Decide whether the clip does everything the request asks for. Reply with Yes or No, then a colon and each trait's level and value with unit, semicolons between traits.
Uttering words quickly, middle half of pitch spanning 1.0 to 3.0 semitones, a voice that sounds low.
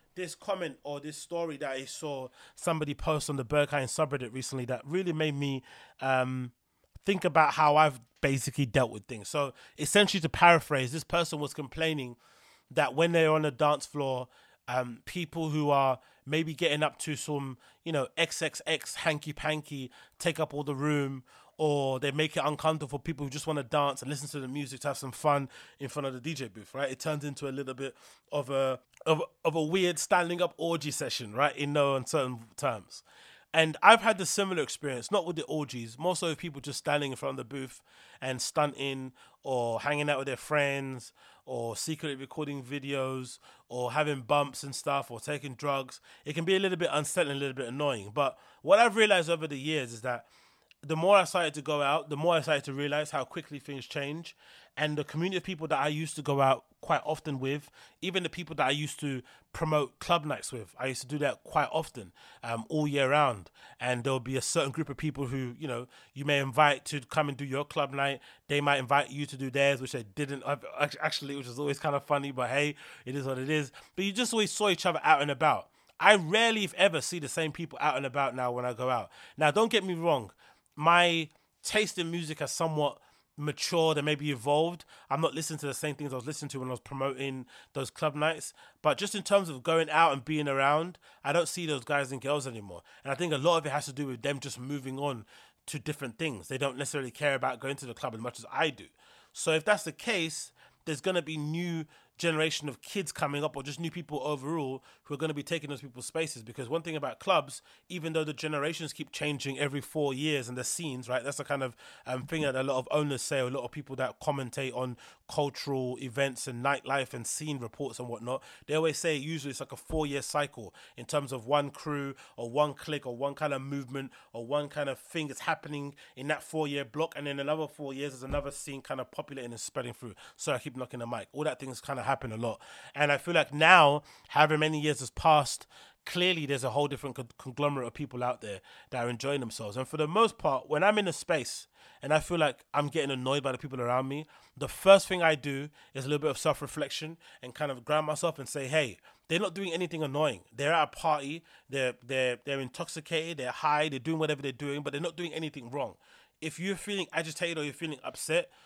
No: fast, 235 wpm; narrow, 2.6 semitones; medium, 145 Hz